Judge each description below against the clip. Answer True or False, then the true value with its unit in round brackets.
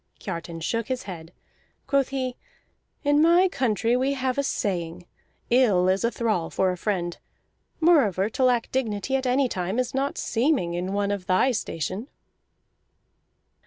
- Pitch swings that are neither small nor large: False (6.2 semitones)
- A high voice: True (225 Hz)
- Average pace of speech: True (155 wpm)